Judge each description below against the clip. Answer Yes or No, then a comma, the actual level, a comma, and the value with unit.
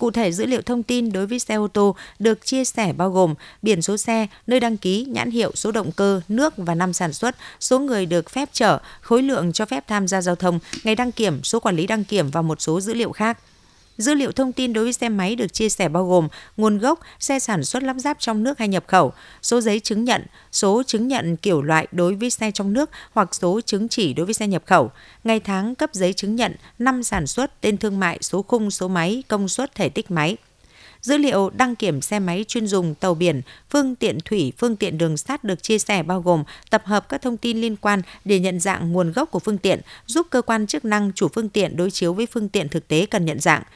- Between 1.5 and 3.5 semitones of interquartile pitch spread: No, average, 4.3 semitones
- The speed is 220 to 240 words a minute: No, fast, 250 wpm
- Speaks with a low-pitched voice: No, high, 210 Hz